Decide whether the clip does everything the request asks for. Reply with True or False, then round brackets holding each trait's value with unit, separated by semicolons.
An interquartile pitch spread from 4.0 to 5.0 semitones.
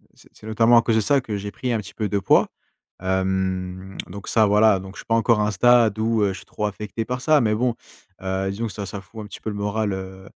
False (2.8 semitones)